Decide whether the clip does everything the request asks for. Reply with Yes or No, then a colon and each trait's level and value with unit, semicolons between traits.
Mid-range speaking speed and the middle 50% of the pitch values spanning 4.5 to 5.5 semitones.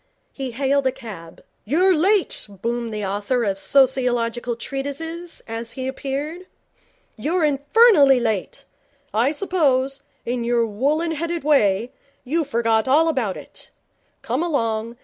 No: slow, 130 wpm; average, 4.9 semitones